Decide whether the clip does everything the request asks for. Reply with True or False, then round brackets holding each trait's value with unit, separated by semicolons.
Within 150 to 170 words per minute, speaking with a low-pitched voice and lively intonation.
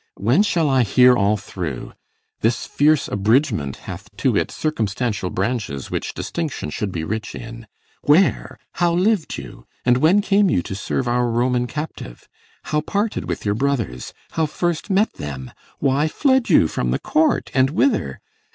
True (160 wpm; 125 Hz; 7.6 semitones)